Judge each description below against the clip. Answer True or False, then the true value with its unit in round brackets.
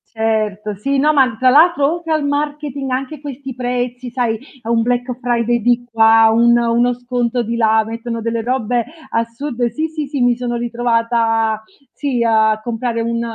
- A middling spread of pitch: False (2.2 semitones)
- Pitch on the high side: True (240 Hz)